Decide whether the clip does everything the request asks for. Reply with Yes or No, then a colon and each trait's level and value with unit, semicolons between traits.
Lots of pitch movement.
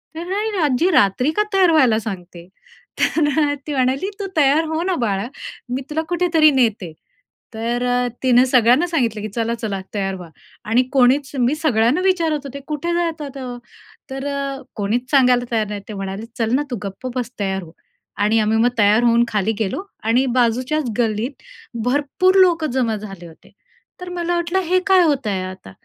Yes: wide, 6.1 semitones